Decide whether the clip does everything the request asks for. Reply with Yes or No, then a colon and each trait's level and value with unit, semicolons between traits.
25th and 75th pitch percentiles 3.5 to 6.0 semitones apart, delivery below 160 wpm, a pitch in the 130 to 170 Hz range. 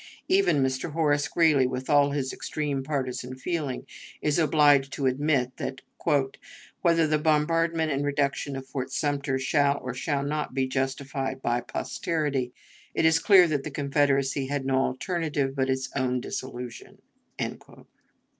No: narrow, 2.4 semitones; average, 145 wpm; medium, 140 Hz